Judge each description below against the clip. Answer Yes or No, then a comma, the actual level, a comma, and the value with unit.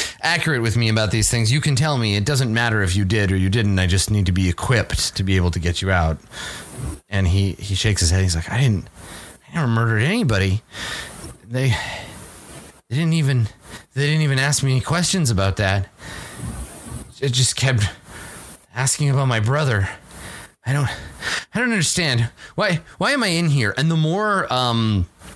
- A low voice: Yes, low, 115 Hz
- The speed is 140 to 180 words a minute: No, average, 190 wpm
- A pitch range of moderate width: No, wide, 6.5 semitones